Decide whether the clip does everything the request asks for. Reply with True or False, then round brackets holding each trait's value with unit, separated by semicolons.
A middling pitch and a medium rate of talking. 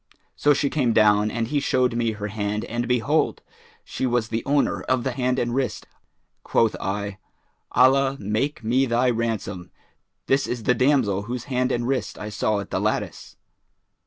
False (120 Hz; 175 wpm)